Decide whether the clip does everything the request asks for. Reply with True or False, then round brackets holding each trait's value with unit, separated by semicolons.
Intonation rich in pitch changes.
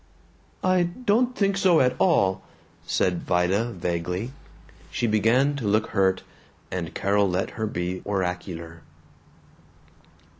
True (8.0 semitones)